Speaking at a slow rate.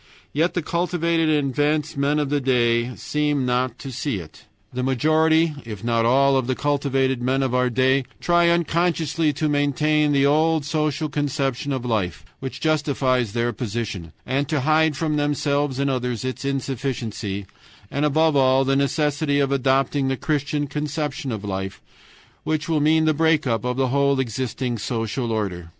No: average, 170 wpm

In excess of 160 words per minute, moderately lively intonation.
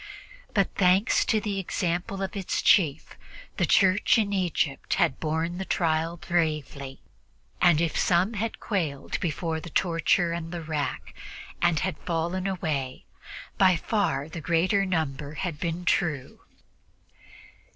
No: slow, 135 wpm; average, 3.1 semitones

